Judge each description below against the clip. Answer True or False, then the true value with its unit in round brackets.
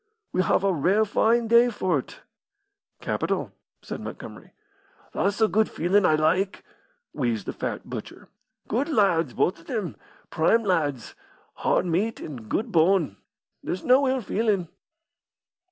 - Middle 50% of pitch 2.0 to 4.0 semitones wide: False (5.5 semitones)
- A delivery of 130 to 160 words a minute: True (135 wpm)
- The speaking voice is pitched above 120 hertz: True (190 Hz)